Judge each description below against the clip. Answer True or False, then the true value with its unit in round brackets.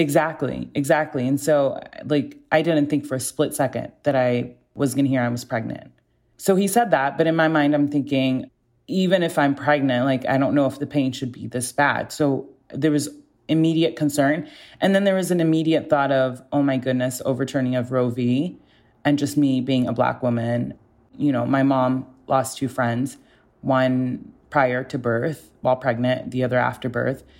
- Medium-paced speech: True (195 wpm)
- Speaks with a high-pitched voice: False (135 Hz)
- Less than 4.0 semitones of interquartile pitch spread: True (2.7 semitones)